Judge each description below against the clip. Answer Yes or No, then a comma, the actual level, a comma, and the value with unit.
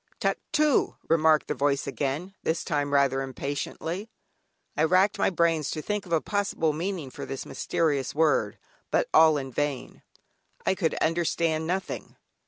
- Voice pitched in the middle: Yes, medium, 160 Hz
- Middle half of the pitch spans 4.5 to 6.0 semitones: No, average, 3.4 semitones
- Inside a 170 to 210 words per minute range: No, average, 150 wpm